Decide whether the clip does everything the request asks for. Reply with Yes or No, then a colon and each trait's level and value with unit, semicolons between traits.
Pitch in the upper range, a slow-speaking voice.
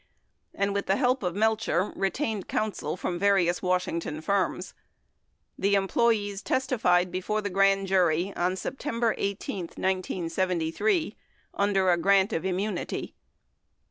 Yes: high, 195 Hz; slow, 120 wpm